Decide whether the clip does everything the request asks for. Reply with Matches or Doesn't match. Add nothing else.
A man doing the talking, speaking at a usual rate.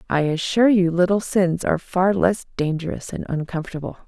Doesn't match